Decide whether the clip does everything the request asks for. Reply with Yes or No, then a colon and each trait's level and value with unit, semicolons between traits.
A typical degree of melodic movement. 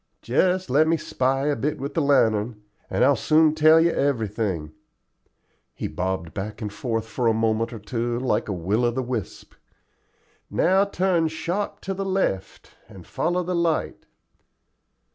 No: wide, 6.8 semitones